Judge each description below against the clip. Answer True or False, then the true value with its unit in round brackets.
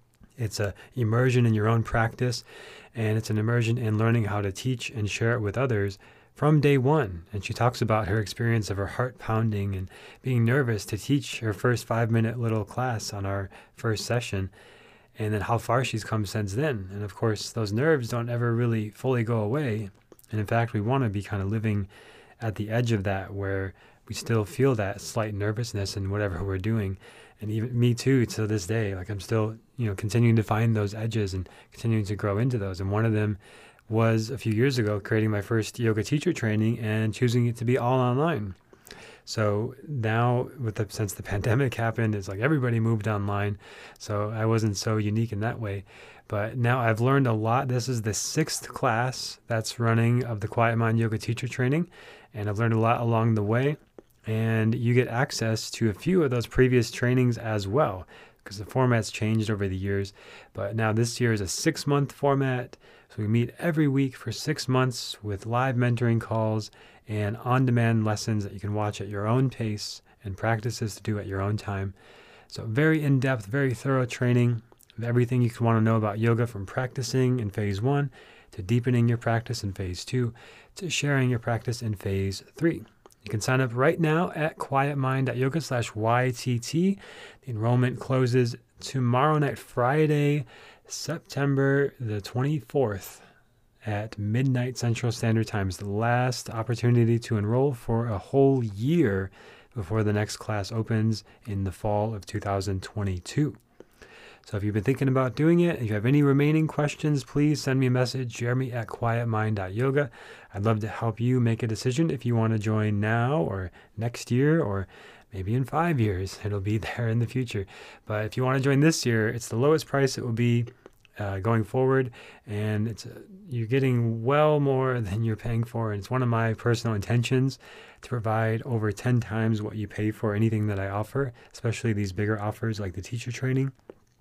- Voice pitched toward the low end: True (115 Hz)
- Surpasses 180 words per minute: True (195 wpm)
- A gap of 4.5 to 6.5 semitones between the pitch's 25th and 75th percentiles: False (3.0 semitones)